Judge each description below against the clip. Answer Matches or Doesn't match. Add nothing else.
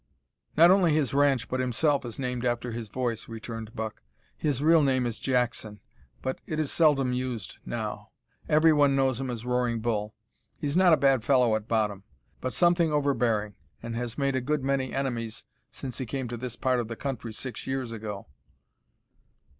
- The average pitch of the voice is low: Matches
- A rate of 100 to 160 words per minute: Doesn't match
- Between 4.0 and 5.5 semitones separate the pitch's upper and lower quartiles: Doesn't match